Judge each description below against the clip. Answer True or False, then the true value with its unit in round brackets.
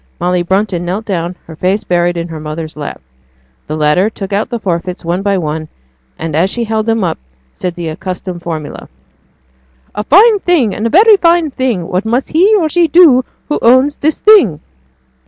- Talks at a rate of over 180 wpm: True (190 wpm)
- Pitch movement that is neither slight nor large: False (7.2 semitones)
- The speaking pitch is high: True (195 Hz)